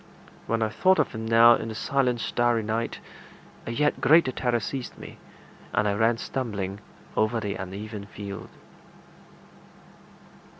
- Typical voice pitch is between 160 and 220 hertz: No, low, 115 Hz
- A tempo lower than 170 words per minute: Yes, average, 140 wpm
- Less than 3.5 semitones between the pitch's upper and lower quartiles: Yes, narrow, 2.4 semitones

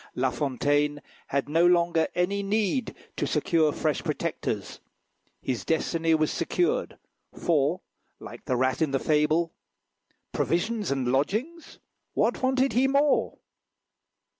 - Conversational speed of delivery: No, slow, 120 wpm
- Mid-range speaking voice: Yes, medium, 165 Hz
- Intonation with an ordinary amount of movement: No, wide, 6.7 semitones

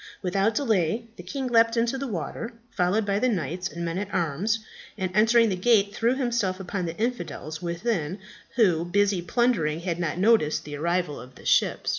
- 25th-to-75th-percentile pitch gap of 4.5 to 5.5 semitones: Yes, average, 4.9 semitones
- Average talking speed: Yes, average, 185 wpm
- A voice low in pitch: No, high, 195 Hz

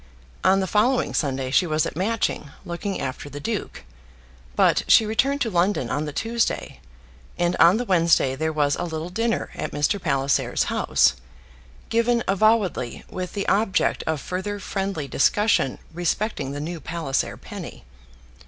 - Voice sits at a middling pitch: Yes, medium, 180 Hz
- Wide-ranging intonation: Yes, wide, 6.0 semitones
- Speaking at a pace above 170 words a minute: No, average, 155 wpm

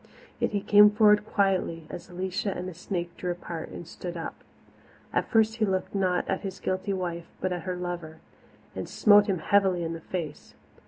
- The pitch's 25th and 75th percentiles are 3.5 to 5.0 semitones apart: No, narrow, 2.6 semitones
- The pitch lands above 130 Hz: Yes, medium, 185 Hz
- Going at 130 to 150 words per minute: No, average, 195 wpm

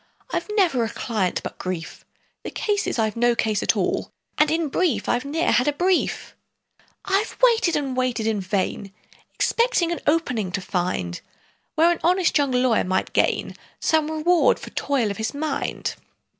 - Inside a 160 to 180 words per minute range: Yes, average, 170 wpm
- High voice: Yes, very high, 265 Hz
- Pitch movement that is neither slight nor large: No, wide, 7.4 semitones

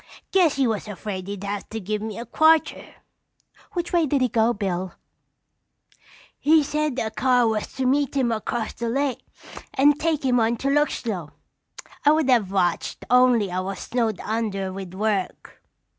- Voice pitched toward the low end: No, high, 230 Hz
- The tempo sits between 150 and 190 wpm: Yes, average, 170 wpm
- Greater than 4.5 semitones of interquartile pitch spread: Yes, average, 5.3 semitones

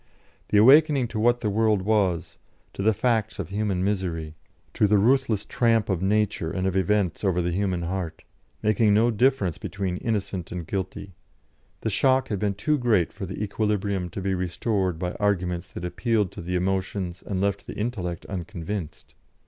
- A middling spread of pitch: Yes, average, 3.0 semitones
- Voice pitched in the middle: No, low, 100 Hz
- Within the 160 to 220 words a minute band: Yes, average, 175 wpm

